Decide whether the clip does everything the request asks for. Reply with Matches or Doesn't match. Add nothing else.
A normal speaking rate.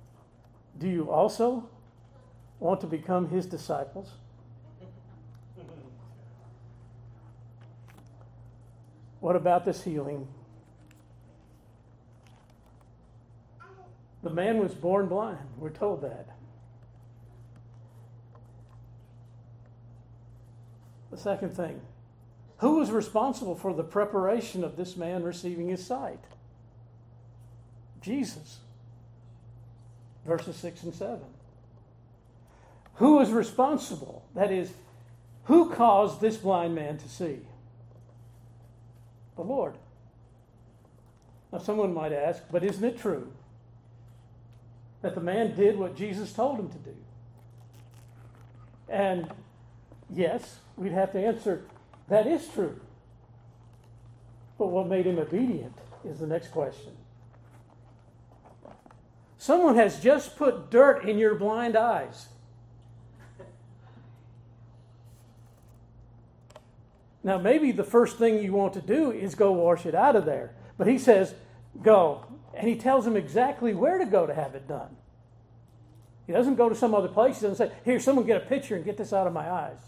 Doesn't match